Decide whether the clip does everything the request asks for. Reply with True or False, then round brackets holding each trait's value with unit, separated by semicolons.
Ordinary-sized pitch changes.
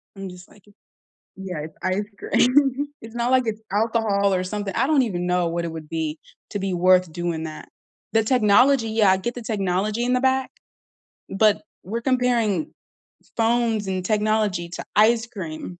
True (4.4 semitones)